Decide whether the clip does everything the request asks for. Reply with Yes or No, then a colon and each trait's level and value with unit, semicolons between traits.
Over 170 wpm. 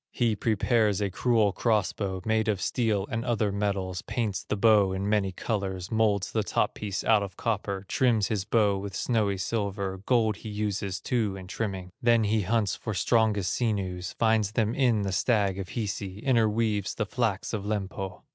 Yes: average, 180 wpm